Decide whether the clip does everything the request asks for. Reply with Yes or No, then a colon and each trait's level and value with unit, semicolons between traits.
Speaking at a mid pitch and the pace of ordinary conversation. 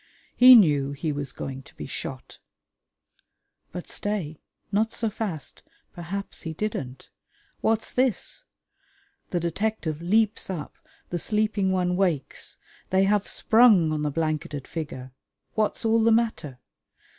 No: medium, 180 Hz; slow, 130 wpm